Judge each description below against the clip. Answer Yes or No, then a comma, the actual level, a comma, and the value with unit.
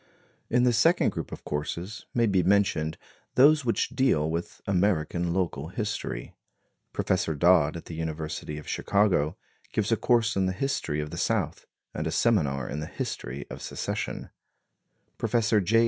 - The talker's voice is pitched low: Yes, very low, 90 Hz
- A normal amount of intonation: No, wide, 6.2 semitones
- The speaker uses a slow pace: No, average, 160 wpm